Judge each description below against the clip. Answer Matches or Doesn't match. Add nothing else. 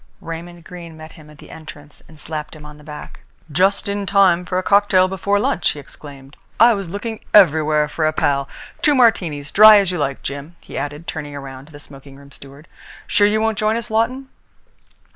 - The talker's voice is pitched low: Doesn't match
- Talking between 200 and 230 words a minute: Matches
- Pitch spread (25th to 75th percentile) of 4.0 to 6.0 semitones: Matches